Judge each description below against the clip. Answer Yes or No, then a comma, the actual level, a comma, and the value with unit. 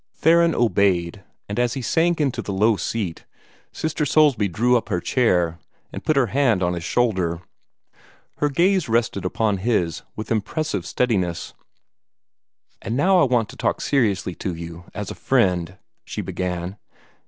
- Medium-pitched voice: No, low, 110 Hz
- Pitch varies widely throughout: Yes, wide, 6.6 semitones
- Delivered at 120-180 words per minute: Yes, average, 155 wpm